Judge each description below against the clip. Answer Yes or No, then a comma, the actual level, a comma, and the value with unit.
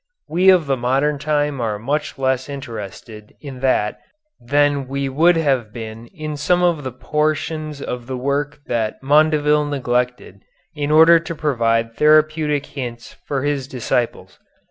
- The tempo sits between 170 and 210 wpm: No, average, 145 wpm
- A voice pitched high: No, medium, 140 Hz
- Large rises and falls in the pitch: No, average, 3.4 semitones